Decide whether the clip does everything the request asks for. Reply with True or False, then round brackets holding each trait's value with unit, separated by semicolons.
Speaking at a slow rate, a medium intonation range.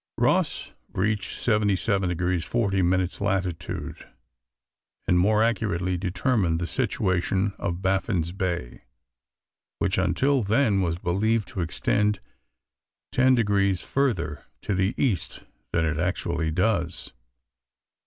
True (110 wpm; 3.3 semitones)